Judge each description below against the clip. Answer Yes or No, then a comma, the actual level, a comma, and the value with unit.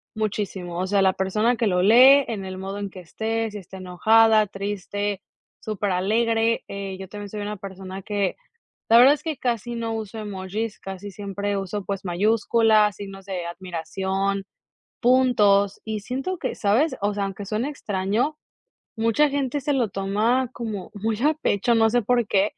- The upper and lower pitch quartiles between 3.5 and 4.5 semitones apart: No, average, 2.8 semitones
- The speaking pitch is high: Yes, high, 205 Hz